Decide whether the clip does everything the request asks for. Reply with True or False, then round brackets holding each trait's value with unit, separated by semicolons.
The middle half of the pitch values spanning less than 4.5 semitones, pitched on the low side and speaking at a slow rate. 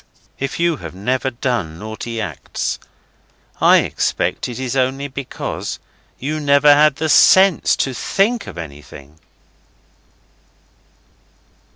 False (5.1 semitones; 130 Hz; 110 wpm)